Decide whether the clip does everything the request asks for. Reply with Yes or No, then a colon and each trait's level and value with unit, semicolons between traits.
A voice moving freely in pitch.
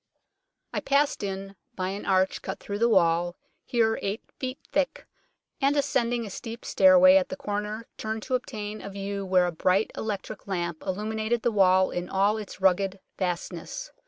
No: average, 3.7 semitones